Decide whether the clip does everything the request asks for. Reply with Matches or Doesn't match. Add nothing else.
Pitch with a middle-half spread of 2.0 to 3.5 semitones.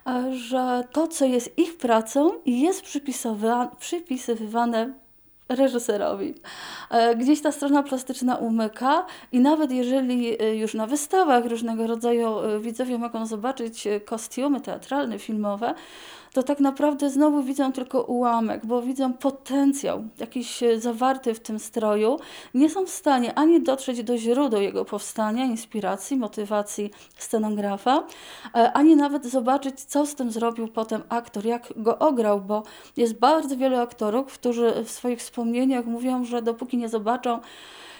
Matches